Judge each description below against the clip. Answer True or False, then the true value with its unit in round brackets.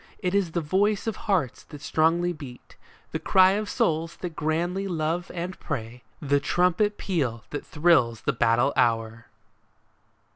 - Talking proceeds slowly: False (150 wpm)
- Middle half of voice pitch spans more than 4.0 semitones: True (4.9 semitones)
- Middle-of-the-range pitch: True (165 Hz)